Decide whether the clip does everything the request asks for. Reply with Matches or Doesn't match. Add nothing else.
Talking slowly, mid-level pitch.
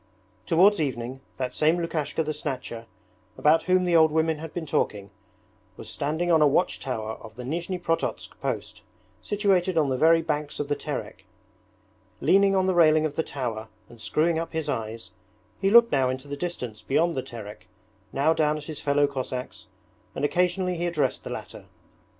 Doesn't match